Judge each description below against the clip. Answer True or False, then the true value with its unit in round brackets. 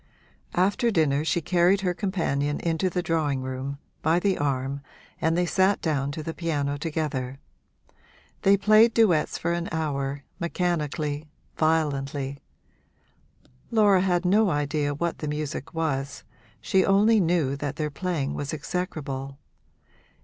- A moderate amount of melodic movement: True (4.0 semitones)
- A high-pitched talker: False (160 Hz)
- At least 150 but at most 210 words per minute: False (135 wpm)